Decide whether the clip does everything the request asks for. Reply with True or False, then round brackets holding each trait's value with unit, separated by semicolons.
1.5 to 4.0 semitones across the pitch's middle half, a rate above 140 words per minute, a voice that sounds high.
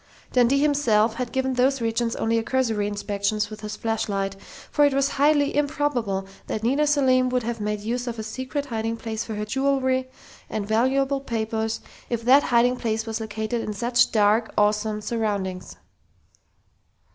True (3.3 semitones; 165 wpm; 230 Hz)